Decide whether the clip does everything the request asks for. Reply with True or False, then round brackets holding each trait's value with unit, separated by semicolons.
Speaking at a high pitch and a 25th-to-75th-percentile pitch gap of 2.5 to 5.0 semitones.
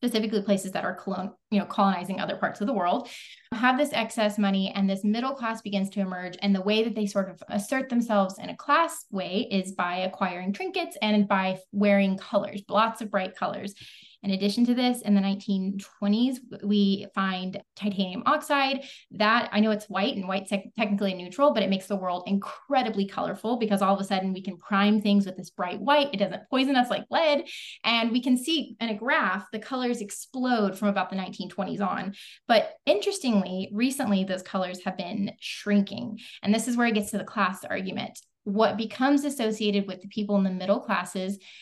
True (205 Hz; 2.9 semitones)